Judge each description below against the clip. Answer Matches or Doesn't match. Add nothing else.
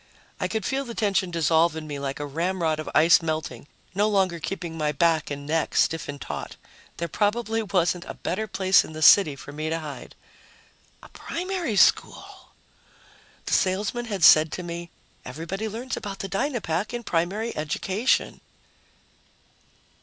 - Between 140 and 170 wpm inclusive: Matches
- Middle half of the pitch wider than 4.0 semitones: Matches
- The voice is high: Doesn't match